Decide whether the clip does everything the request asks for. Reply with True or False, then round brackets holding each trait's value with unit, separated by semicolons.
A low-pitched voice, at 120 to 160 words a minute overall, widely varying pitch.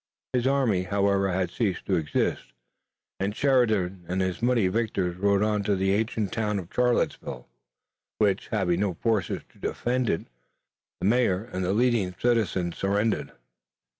False (100 Hz; 150 wpm; 3.6 semitones)